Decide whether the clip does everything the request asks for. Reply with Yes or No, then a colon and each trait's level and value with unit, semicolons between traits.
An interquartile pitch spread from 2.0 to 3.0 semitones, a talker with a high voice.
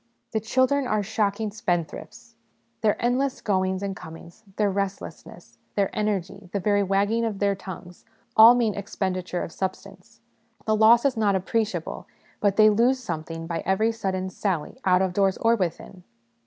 Yes: average, 2.7 semitones; high, 200 Hz